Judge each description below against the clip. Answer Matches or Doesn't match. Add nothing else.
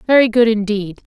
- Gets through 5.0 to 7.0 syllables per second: Matches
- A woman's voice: Matches